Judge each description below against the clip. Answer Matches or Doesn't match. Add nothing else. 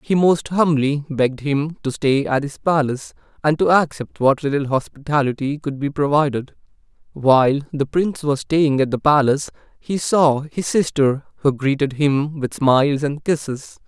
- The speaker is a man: Matches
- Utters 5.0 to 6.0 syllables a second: Doesn't match